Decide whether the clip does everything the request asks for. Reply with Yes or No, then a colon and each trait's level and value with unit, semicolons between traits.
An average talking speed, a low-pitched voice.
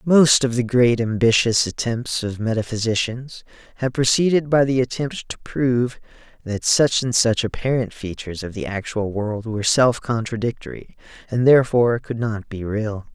Yes: average, 155 wpm; low, 115 Hz